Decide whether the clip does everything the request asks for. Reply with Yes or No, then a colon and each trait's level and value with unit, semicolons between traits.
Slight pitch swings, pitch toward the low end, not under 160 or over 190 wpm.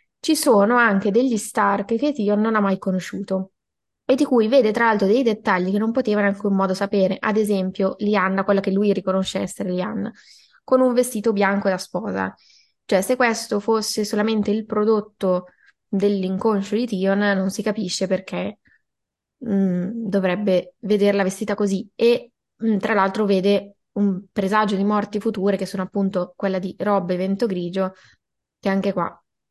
No: narrow, 2.3 semitones; high, 205 Hz; average, 165 wpm